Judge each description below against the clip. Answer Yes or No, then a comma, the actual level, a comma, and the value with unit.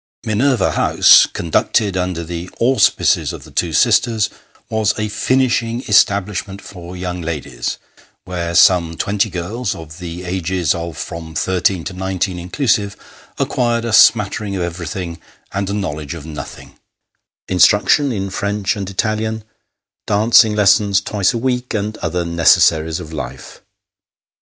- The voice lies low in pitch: Yes, very low, 95 Hz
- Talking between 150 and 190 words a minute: No, slow, 135 wpm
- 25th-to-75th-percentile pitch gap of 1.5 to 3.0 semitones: No, average, 3.9 semitones